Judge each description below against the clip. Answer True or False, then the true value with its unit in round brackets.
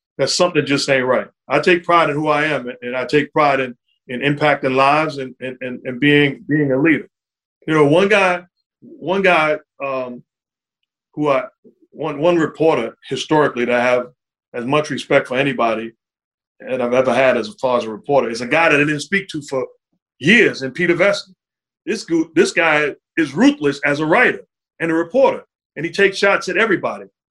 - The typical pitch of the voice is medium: True (145 Hz)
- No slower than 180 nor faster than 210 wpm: True (200 wpm)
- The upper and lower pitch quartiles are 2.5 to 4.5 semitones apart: False (5.0 semitones)